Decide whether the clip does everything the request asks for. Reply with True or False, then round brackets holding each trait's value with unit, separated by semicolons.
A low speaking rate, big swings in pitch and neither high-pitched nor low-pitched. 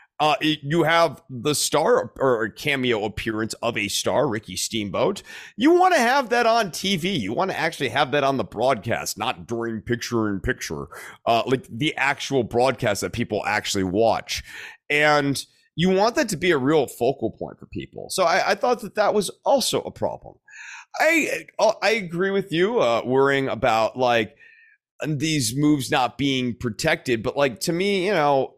False (175 wpm; 7.7 semitones; 145 Hz)